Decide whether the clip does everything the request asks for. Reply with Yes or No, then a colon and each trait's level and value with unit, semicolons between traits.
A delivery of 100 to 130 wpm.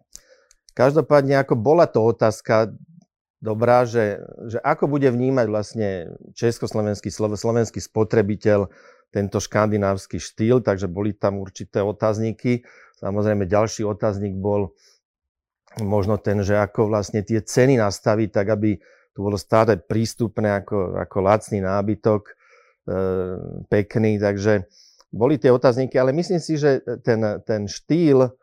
Yes: average, 120 wpm